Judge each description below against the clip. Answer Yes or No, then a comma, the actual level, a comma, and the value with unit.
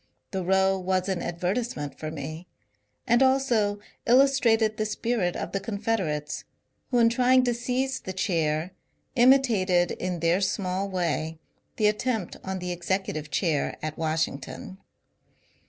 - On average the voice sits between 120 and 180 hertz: No, high, 190 Hz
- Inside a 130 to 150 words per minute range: Yes, average, 140 wpm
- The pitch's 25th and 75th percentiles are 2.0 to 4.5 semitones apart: No, average, 5.0 semitones